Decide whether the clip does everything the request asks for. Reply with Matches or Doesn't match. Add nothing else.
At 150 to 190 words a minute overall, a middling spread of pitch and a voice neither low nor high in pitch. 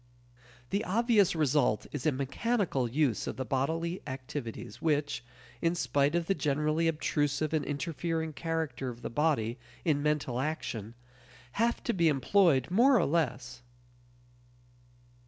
Doesn't match